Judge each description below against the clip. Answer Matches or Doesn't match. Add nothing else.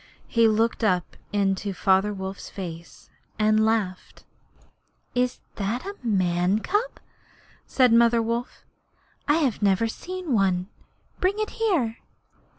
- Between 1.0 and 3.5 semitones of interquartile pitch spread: Doesn't match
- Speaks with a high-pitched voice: Matches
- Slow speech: Matches